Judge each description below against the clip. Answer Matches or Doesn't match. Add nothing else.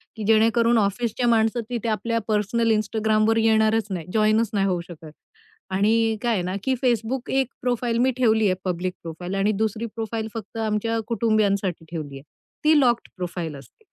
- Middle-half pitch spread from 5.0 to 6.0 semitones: Doesn't match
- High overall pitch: Matches